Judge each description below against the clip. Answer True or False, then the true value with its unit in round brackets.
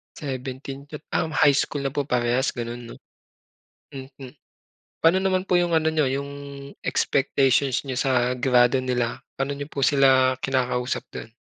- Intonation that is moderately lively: False (2.0 semitones)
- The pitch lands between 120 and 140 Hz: True (135 Hz)